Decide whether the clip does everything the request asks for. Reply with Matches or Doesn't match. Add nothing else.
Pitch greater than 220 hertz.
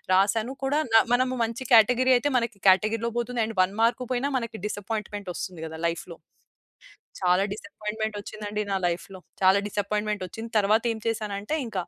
Doesn't match